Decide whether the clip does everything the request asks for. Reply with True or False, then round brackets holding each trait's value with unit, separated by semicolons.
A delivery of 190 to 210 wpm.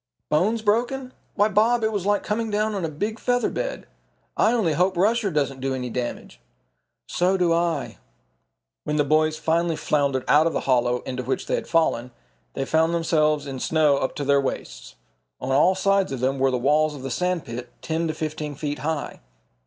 True (200 wpm)